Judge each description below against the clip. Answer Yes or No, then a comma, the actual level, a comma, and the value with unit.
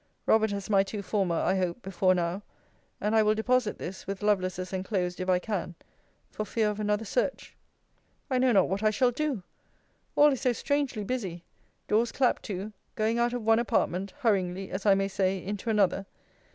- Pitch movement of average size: Yes, average, 3.0 semitones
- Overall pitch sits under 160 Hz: No, high, 205 Hz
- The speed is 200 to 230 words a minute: No, average, 190 wpm